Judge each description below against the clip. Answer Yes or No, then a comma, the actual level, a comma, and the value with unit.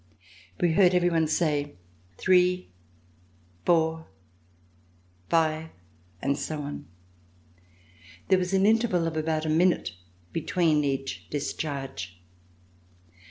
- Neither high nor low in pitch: Yes, medium, 160 Hz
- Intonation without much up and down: No, average, 3.3 semitones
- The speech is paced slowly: Yes, slow, 95 wpm